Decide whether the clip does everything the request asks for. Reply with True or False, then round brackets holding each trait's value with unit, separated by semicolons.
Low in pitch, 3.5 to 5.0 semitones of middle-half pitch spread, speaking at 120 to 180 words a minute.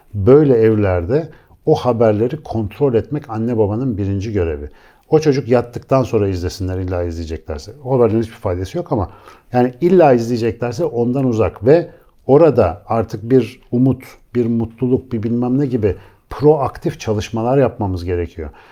True (115 Hz; 4.2 semitones; 140 wpm)